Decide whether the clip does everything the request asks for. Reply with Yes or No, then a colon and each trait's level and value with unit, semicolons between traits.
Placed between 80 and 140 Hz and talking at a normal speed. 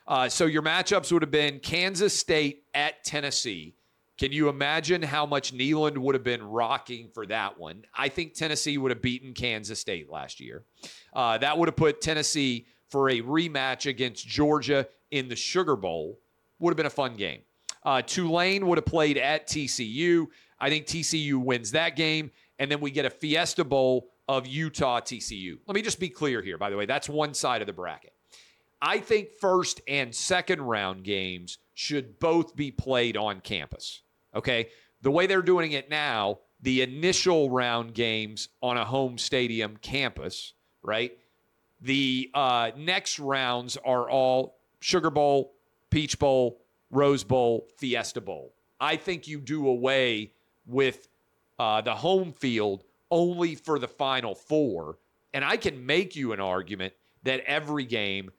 Yes: low, 135 Hz; average, 165 wpm